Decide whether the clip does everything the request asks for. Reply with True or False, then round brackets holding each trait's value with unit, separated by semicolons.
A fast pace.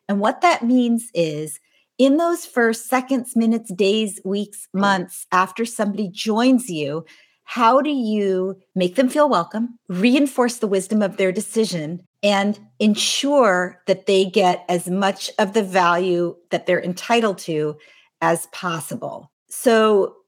False (140 wpm)